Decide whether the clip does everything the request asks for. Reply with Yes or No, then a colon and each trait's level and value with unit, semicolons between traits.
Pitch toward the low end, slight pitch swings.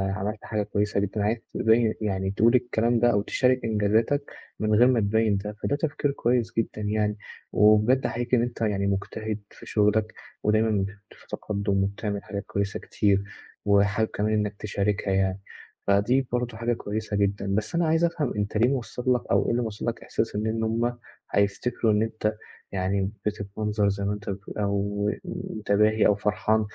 Yes: low, 105 Hz; narrow, 2.1 semitones